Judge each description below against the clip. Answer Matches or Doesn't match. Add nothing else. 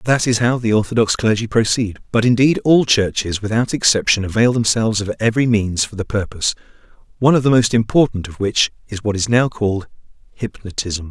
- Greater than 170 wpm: Matches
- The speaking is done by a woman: Doesn't match